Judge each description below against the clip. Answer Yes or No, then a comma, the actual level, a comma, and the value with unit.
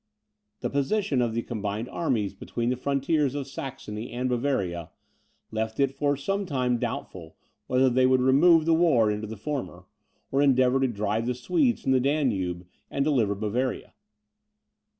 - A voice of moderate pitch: No, low, 130 Hz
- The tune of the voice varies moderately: Yes, average, 4.1 semitones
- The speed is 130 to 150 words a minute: No, average, 160 wpm